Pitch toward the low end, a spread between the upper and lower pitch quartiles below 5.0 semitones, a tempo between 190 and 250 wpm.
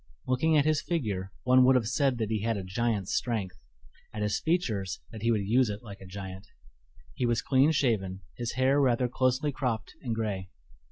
Yes: low, 115 Hz; average, 4.2 semitones; average, 200 wpm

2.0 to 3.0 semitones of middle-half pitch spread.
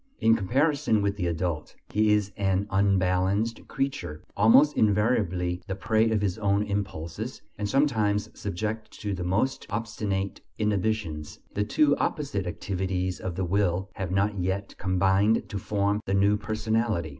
Yes: narrow, 2.6 semitones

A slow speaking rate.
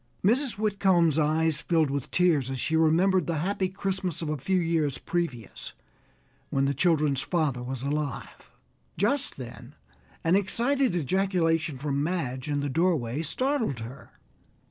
No: average, 145 wpm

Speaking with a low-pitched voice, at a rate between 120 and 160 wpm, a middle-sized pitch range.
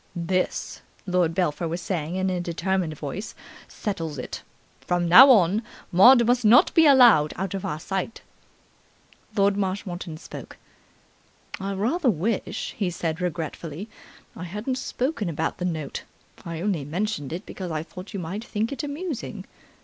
No: medium, 185 Hz; average, 150 wpm; average, 4.3 semitones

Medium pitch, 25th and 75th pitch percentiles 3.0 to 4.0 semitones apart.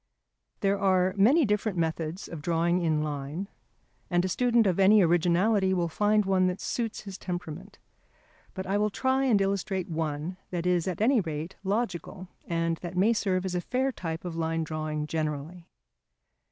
Yes: medium, 180 Hz; average, 3.4 semitones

